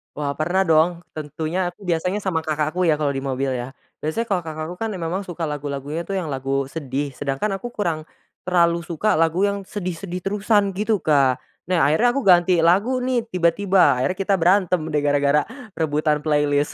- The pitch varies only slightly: No, average, 4.2 semitones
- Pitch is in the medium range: Yes, medium, 165 Hz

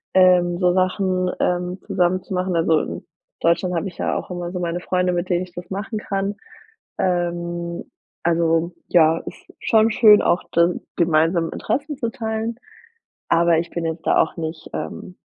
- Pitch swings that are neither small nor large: No, narrow, 1.7 semitones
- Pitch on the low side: No, medium, 175 Hz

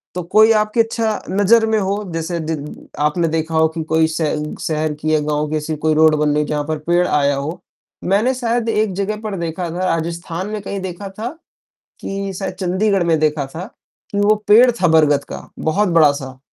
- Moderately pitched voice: Yes, medium, 170 Hz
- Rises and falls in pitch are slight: No, average, 4.5 semitones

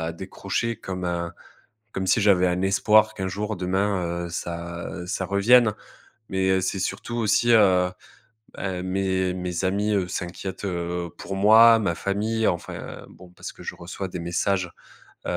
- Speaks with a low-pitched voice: Yes, very low, 95 Hz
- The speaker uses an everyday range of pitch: No, narrow, 2.3 semitones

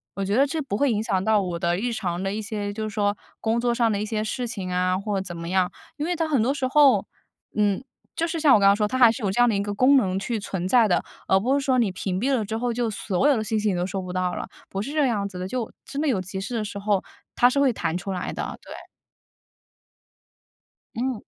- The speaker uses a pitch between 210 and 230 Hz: Yes, high, 215 Hz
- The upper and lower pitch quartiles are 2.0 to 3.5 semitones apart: No, average, 4.3 semitones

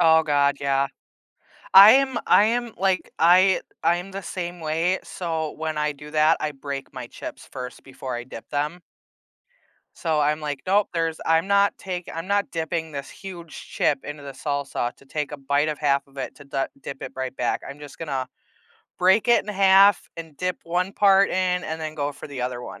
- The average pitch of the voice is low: No, medium, 160 Hz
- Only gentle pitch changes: No, average, 4.4 semitones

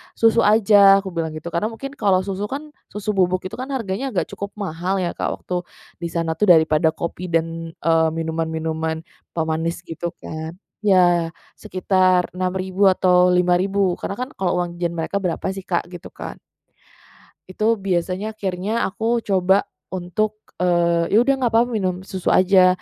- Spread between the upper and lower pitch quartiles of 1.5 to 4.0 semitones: Yes, average, 2.9 semitones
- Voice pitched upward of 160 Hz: Yes, medium, 185 Hz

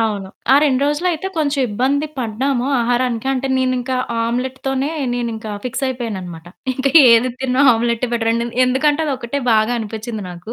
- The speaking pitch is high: Yes, high, 245 Hz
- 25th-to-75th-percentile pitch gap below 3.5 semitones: Yes, average, 2.8 semitones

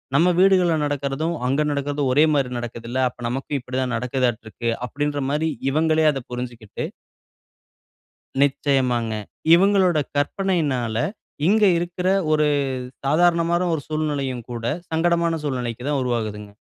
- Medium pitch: Yes, medium, 145 Hz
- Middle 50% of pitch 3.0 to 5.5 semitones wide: Yes, average, 4.7 semitones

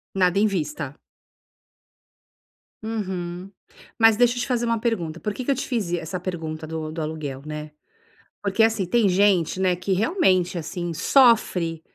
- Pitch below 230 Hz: Yes, medium, 185 Hz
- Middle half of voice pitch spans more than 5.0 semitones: Yes, wide, 5.4 semitones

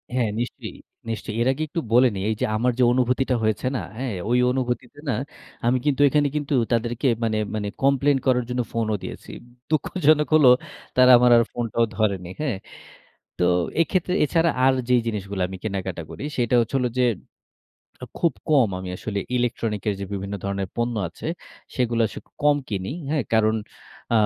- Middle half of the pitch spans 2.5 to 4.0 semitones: Yes, average, 3.6 semitones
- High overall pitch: No, low, 120 Hz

